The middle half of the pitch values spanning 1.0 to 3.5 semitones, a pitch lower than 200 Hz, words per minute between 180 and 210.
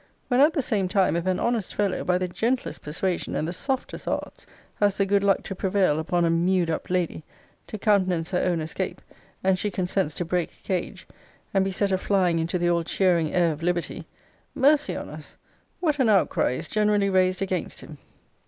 Yes: average, 2.7 semitones; medium, 185 Hz; average, 200 wpm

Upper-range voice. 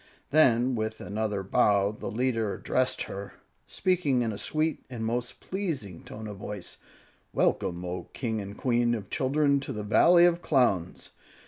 No: low, 115 Hz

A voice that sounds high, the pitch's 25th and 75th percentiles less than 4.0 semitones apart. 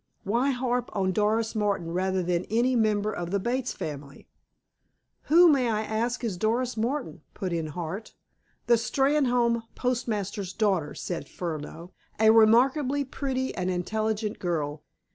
No: high, 215 Hz; average, 5.0 semitones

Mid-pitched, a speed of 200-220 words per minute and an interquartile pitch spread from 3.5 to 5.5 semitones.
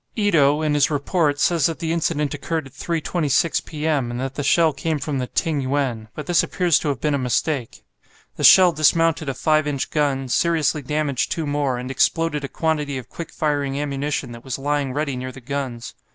No: medium, 145 Hz; fast, 205 wpm; average, 2.8 semitones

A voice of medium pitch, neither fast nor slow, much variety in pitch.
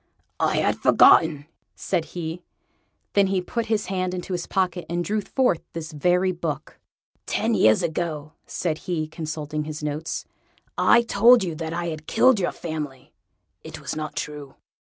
No: medium, 170 Hz; average, 160 wpm; average, 3.1 semitones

